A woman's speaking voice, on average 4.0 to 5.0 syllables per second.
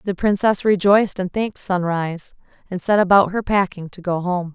No: female; 5.4 syllables/s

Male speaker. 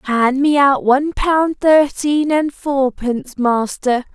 No: female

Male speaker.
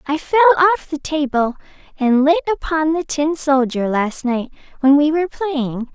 No: female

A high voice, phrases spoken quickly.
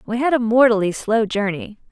No: high, 225 Hz; average, 190 wpm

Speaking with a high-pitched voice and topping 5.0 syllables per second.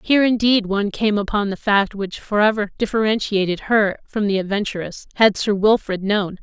Yes: high, 205 Hz; 5.3 syllables/s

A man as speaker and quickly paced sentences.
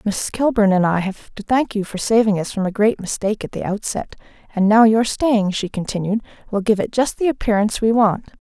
No: female; fast, 230 wpm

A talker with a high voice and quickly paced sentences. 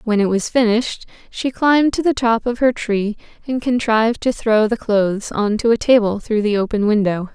Yes: high, 225 Hz; fast, 210 wpm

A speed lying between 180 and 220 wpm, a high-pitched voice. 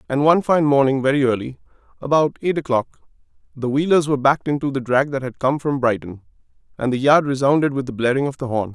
No: average, 200 wpm; low, 135 Hz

